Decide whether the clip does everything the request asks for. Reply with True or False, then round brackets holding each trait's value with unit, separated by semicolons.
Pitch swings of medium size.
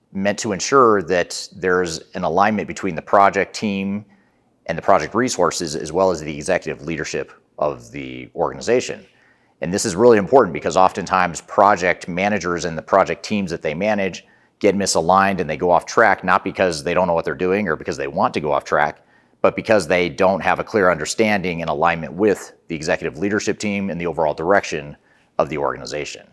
False (2.2 semitones)